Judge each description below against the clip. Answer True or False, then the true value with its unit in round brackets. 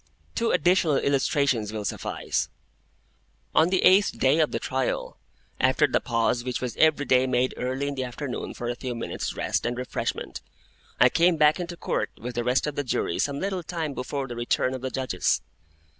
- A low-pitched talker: True (130 Hz)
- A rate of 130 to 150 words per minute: False (190 wpm)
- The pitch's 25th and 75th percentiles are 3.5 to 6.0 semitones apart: True (3.8 semitones)